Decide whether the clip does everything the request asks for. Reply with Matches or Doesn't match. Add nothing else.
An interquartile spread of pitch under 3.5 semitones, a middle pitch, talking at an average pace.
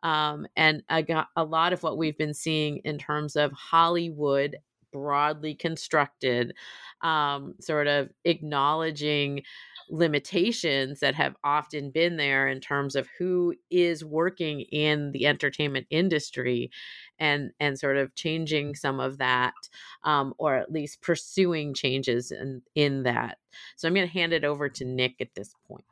Matches